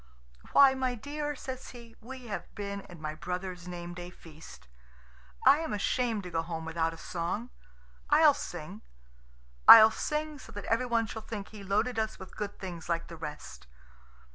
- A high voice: Yes, high, 200 Hz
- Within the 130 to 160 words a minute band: No, average, 170 wpm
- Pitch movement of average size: No, wide, 5.8 semitones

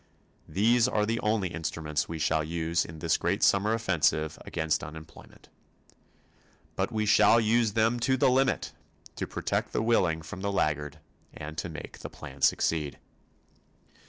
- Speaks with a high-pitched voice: No, very low, 85 Hz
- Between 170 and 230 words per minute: No, average, 155 wpm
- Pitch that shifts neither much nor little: No, wide, 6.1 semitones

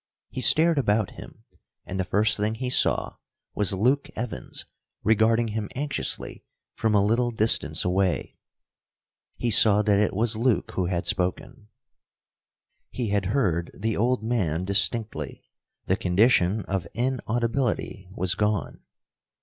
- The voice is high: No, low, 110 Hz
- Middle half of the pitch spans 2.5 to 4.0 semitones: Yes, average, 3.6 semitones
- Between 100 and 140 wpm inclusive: Yes, slow, 135 wpm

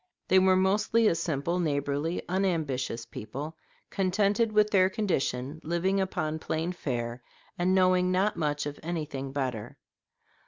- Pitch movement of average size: Yes, average, 4.8 semitones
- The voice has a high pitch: No, medium, 170 Hz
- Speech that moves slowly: Yes, slow, 130 wpm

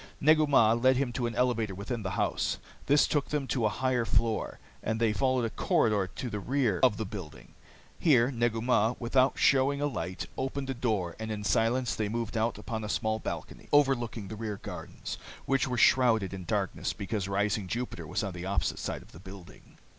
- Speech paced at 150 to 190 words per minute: No, fast, 205 wpm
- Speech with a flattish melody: No, average, 3.9 semitones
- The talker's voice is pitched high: No, low, 115 Hz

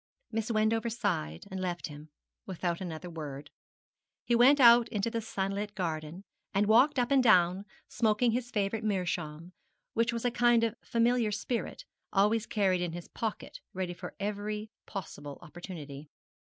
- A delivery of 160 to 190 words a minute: No, average, 150 wpm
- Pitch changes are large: No, average, 4.7 semitones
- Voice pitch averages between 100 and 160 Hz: No, high, 205 Hz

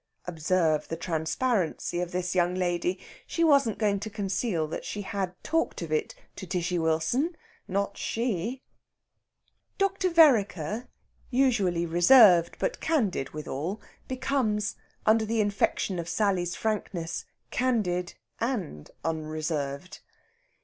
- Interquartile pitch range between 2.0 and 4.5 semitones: No, average, 5.1 semitones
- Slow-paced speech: Yes, slow, 115 wpm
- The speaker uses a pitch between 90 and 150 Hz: No, high, 190 Hz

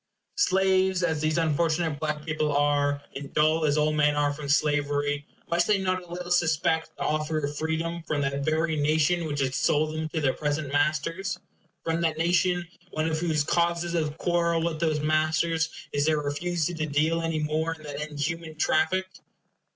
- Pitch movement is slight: Yes, narrow, 2.1 semitones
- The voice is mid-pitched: Yes, medium, 155 Hz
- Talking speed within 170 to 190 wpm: Yes, average, 180 wpm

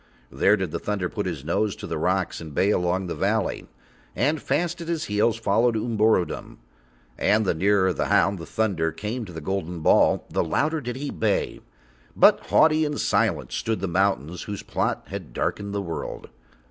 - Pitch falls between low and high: No, low, 100 Hz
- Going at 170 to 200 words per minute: Yes, average, 185 wpm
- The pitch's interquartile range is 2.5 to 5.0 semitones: Yes, average, 4.2 semitones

